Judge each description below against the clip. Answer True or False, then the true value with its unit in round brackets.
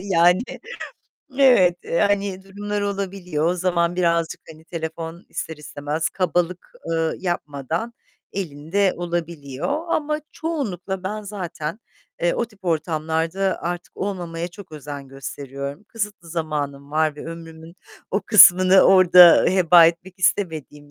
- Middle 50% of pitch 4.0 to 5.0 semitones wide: False (3.3 semitones)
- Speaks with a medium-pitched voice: True (175 Hz)